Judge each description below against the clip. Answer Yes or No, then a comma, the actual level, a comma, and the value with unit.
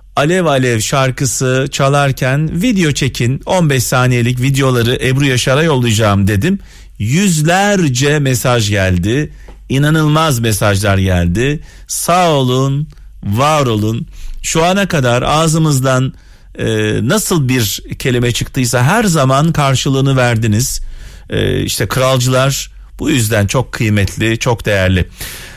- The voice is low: Yes, low, 130 Hz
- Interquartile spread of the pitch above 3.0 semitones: Yes, average, 4.6 semitones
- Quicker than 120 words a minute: No, average, 105 wpm